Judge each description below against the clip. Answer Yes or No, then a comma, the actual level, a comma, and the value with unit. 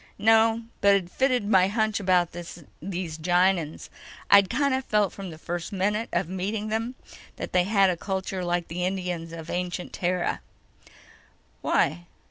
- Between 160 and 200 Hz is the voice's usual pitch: Yes, medium, 185 Hz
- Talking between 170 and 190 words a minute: No, average, 155 wpm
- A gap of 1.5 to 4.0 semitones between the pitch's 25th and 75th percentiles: Yes, average, 3.1 semitones